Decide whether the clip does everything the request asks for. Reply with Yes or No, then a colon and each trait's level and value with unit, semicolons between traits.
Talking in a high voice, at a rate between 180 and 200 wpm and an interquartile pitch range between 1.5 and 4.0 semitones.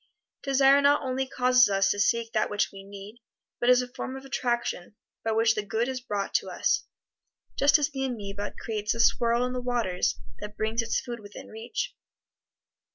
Yes: high, 235 Hz; average, 190 wpm; average, 3.5 semitones